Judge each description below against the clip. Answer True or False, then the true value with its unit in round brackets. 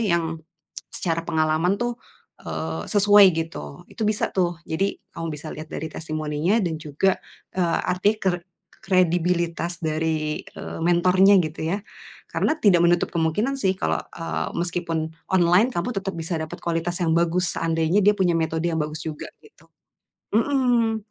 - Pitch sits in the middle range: True (170 Hz)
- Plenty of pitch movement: False (3.2 semitones)